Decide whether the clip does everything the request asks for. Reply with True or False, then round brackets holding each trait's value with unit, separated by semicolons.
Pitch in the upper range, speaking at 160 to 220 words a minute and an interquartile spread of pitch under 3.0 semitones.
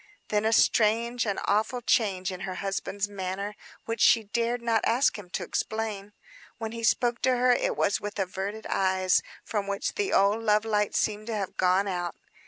True (210 Hz; 190 wpm; 2.6 semitones)